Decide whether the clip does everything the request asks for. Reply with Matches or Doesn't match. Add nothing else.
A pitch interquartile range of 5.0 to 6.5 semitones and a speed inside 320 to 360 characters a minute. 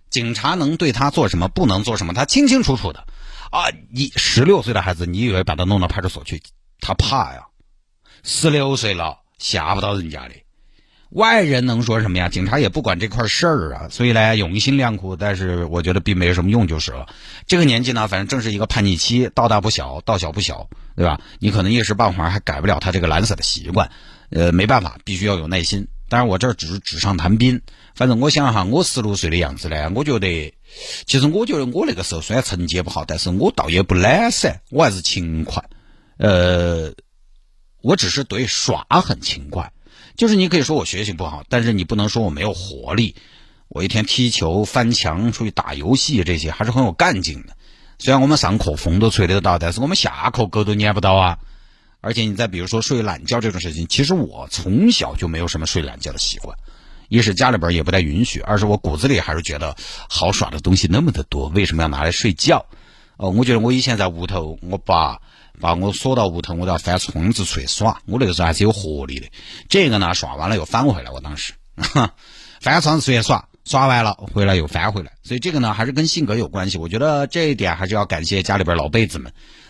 Matches